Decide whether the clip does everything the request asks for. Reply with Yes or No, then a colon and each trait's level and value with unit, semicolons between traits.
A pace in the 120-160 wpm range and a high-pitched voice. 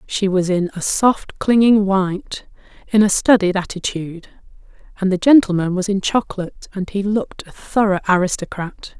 Yes: average, 155 wpm; high, 195 Hz